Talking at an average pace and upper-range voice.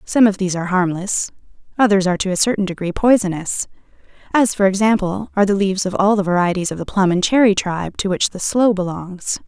No: fast, 210 wpm; high, 195 Hz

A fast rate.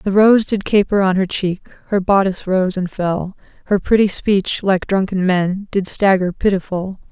No: average, 175 wpm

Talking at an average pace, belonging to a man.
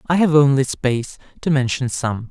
Yes: average, 180 wpm; male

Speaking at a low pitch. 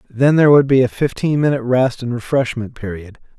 Yes: low, 125 Hz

